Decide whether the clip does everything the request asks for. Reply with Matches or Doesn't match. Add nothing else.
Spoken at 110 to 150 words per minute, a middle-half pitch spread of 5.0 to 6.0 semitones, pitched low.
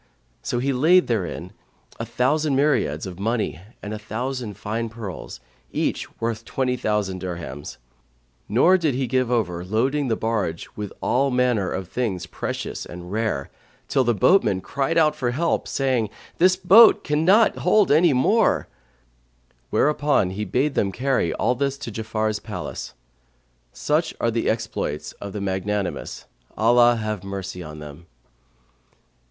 Matches